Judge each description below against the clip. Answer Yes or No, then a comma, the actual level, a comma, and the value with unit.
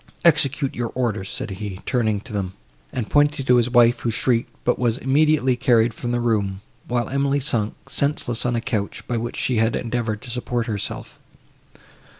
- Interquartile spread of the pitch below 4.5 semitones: Yes, narrow, 2.6 semitones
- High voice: No, low, 120 Hz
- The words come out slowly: No, average, 180 wpm